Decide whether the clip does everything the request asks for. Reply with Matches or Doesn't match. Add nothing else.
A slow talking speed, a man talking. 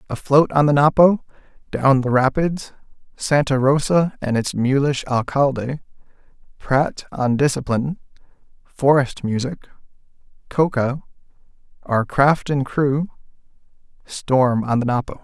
Matches